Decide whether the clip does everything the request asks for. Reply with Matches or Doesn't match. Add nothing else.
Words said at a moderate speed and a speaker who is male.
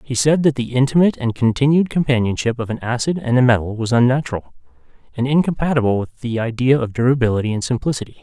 Matches